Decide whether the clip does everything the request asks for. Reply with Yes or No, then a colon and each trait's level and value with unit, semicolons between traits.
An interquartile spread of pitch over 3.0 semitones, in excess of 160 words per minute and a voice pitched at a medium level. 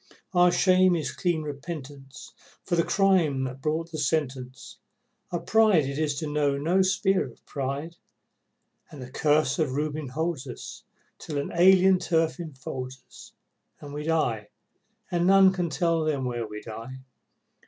No: average, 4.3 semitones; average, 155 wpm; medium, 155 Hz